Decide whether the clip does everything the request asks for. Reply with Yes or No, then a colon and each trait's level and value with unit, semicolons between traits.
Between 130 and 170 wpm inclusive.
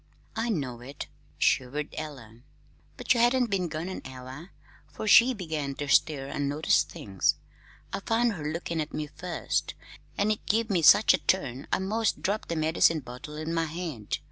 No: average, 180 wpm